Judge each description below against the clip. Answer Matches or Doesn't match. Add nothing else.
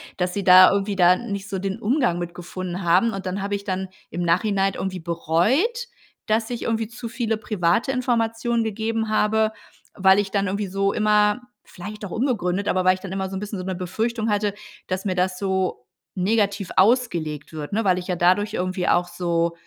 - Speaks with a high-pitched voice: Matches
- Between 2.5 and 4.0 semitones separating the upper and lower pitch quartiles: Matches